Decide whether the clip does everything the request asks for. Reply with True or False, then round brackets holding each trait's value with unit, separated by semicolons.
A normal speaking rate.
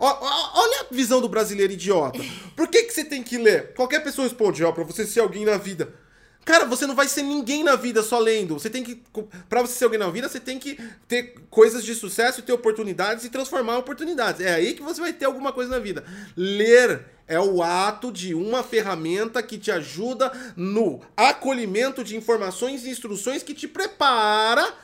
False (205 wpm)